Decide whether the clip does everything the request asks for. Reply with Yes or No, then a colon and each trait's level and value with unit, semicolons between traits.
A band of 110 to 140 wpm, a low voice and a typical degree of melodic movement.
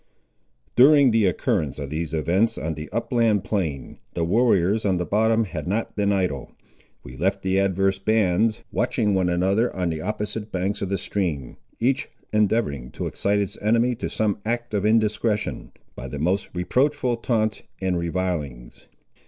No: average, 160 wpm; low, 100 Hz; average, 4.0 semitones